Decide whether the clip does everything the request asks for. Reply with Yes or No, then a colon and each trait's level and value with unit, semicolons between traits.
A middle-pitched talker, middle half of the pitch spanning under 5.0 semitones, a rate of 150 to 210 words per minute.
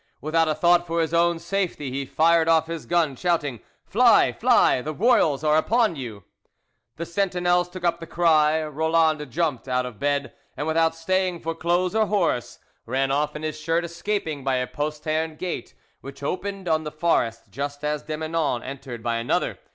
Yes: medium, 160 Hz; average, 3.1 semitones; average, 180 wpm